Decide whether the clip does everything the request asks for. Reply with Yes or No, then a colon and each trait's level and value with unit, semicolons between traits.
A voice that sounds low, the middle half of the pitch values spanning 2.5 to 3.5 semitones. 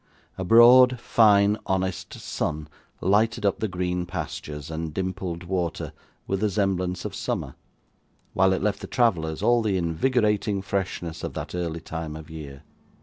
No: very low, 95 Hz; average, 3.9 semitones